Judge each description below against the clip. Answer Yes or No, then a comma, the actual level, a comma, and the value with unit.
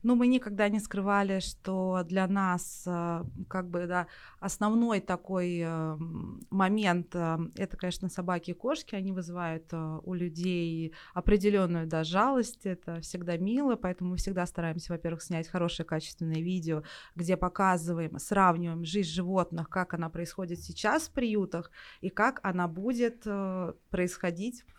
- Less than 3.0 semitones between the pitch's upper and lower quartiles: Yes, narrow, 2.5 semitones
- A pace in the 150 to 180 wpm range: No, average, 135 wpm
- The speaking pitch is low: No, medium, 180 Hz